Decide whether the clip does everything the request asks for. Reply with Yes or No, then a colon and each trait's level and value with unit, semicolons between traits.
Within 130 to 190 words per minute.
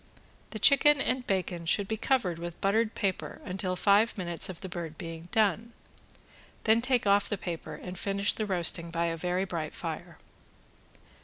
Yes: average, 170 wpm